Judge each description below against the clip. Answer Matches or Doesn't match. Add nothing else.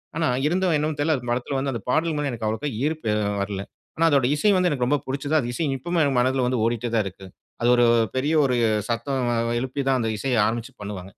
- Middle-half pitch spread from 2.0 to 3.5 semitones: Doesn't match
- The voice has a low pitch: Matches